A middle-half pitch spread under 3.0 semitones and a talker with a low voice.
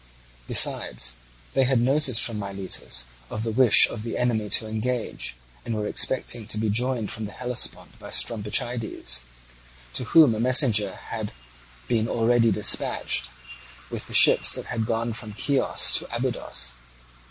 Yes: narrow, 2.6 semitones; low, 115 Hz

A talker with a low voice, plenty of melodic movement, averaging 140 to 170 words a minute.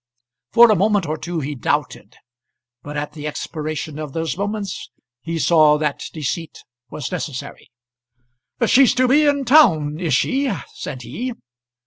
No: medium, 165 Hz; wide, 6.5 semitones; average, 150 wpm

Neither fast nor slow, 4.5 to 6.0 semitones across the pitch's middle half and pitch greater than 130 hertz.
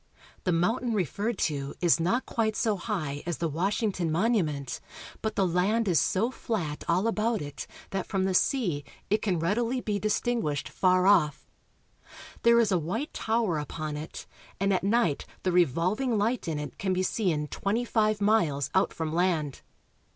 Yes: average, 175 wpm; average, 5.1 semitones; high, 190 Hz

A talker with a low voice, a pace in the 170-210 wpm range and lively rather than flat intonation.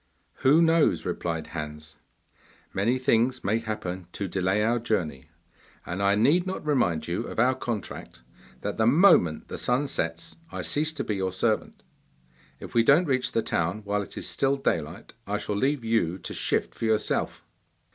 Yes: low, 110 Hz; average, 175 wpm; wide, 6.4 semitones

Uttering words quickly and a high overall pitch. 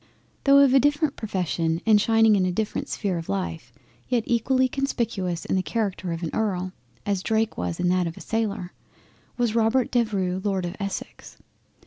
No: average, 175 wpm; high, 205 Hz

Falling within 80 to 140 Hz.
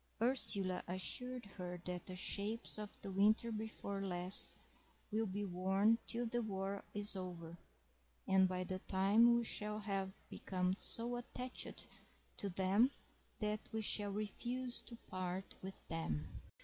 No: high, 200 Hz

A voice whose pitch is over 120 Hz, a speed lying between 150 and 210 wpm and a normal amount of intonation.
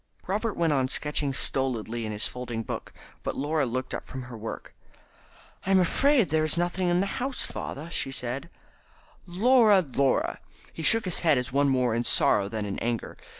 No: medium, 140 Hz; average, 185 wpm; wide, 6.3 semitones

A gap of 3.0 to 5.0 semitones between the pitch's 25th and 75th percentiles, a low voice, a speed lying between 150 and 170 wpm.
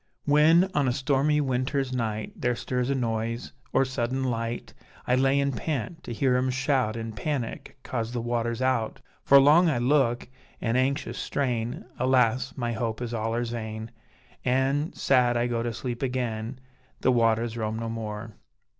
No: narrow, 2.6 semitones; low, 125 Hz; average, 165 wpm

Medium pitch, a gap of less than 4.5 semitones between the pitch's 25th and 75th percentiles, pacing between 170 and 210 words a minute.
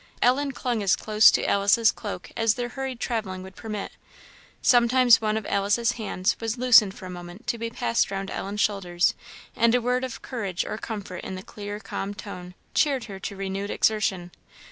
No: high, 210 Hz; average, 3.4 semitones; average, 190 wpm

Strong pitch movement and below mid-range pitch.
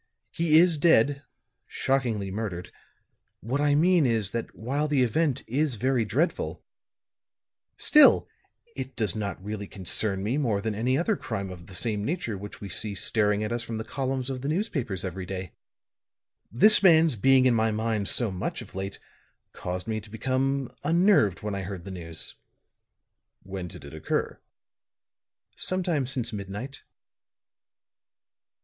Yes: wide, 5.7 semitones; low, 115 Hz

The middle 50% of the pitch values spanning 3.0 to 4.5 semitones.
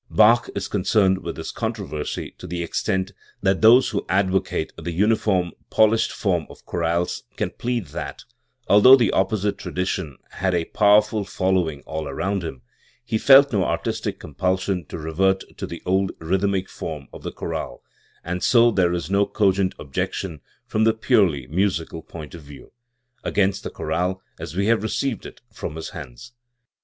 Yes: average, 3.5 semitones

